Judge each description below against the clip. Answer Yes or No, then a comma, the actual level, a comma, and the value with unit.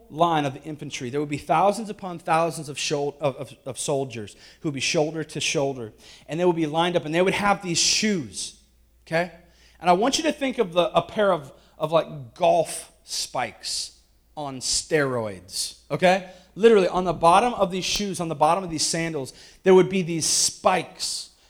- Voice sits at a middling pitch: Yes, medium, 165 Hz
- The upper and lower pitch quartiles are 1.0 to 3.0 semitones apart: No, average, 4.2 semitones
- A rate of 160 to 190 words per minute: No, average, 200 wpm